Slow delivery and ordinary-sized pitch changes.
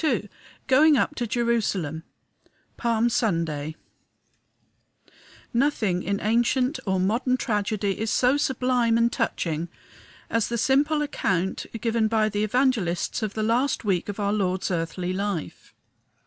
Yes: slow, 130 wpm; average, 4.4 semitones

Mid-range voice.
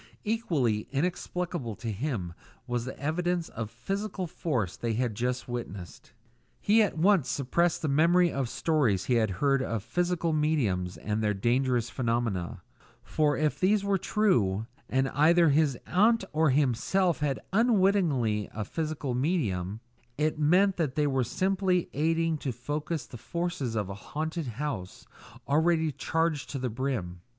Yes: medium, 145 Hz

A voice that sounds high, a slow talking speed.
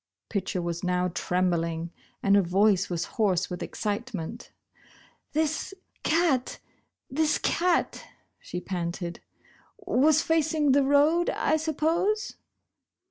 Yes: high, 230 Hz; slow, 110 wpm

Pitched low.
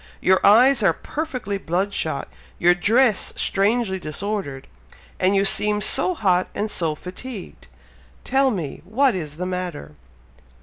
No: high, 195 Hz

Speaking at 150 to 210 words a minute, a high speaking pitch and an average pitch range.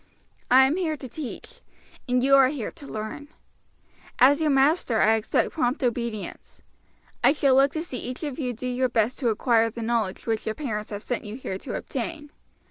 Yes: average, 200 wpm; very high, 250 Hz; average, 3.7 semitones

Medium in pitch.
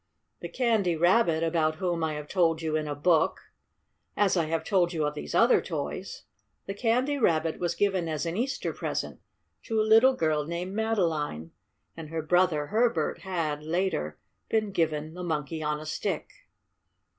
Yes: medium, 170 Hz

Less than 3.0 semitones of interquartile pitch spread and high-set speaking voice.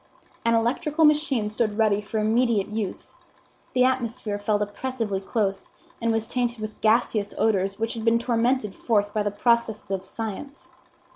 Yes: narrow, 2.5 semitones; high, 225 Hz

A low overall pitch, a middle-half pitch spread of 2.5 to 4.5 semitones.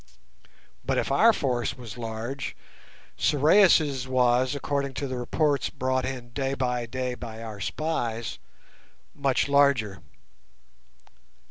Yes: low, 130 Hz; average, 2.8 semitones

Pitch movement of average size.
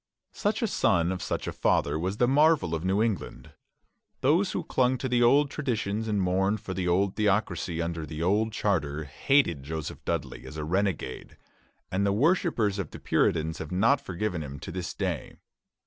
No: wide, 6.0 semitones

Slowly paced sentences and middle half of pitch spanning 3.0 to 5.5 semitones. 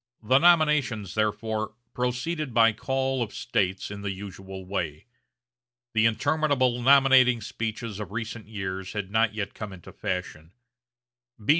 Yes: slow, 130 wpm; average, 4.0 semitones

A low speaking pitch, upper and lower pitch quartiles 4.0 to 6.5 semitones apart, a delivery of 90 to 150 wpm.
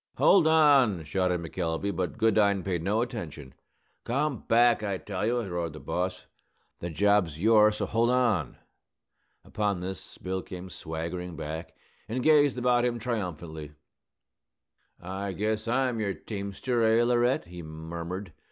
Yes: low, 100 Hz; average, 5.2 semitones; average, 140 wpm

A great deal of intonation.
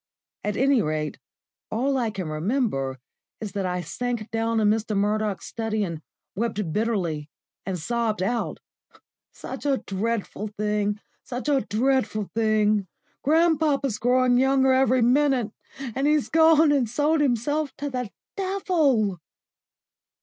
No: average, 4.6 semitones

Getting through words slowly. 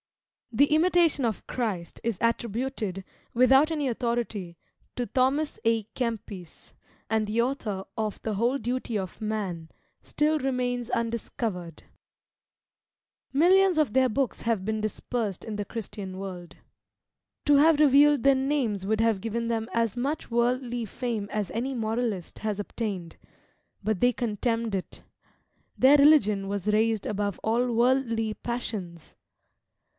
Yes: slow, 130 wpm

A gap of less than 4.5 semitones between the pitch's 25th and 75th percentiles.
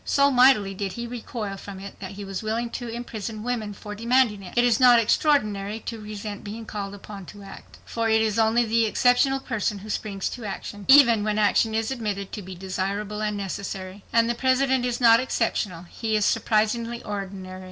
Yes: average, 2.8 semitones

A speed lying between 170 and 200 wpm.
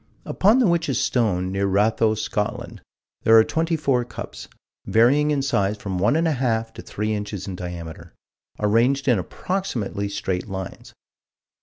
No: average, 155 wpm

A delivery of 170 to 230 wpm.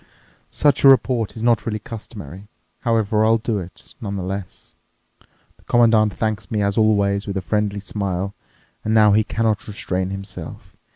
No: average, 155 wpm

